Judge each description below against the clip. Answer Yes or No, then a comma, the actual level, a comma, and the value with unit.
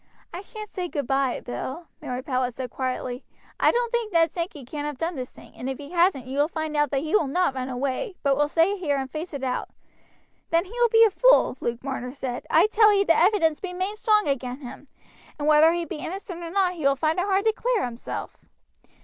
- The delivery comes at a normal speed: No, fast, 235 wpm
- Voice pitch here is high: Yes, very high, 315 Hz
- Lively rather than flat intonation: Yes, wide, 5.9 semitones